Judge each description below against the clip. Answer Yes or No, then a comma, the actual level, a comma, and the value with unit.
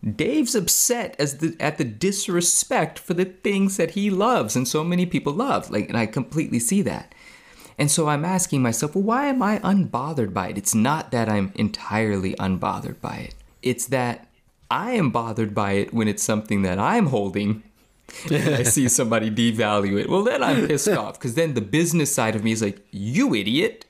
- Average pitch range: No, wide, 8.3 semitones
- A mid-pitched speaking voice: No, low, 130 Hz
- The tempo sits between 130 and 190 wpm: No, average, 200 wpm